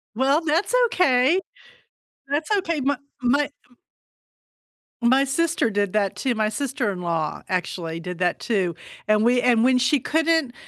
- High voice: Yes, very high, 250 Hz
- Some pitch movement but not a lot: No, wide, 6.1 semitones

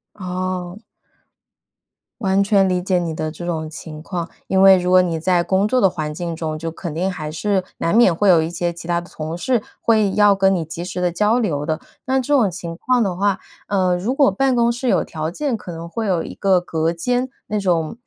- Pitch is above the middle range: No, medium, 180 Hz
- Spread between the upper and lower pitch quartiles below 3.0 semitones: No, average, 3.5 semitones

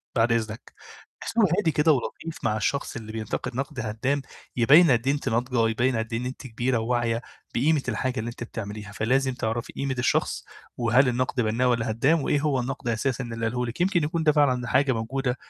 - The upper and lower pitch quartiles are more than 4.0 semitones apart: No, average, 3.2 semitones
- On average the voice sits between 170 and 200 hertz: No, low, 125 Hz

